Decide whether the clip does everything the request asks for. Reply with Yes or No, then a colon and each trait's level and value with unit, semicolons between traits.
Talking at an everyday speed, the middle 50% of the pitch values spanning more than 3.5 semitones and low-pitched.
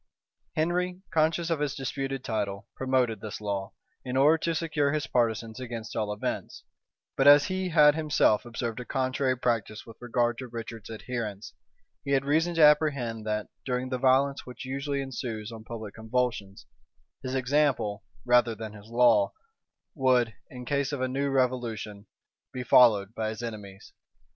Yes: average, 160 wpm; average, 3.9 semitones; low, 125 Hz